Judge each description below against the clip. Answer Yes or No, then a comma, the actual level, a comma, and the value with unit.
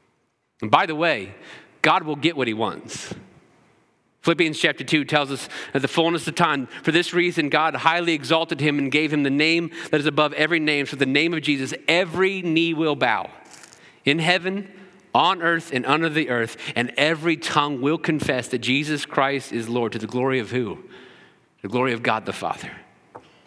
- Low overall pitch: No, medium, 155 Hz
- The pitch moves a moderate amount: Yes, average, 3.2 semitones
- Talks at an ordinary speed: Yes, average, 190 wpm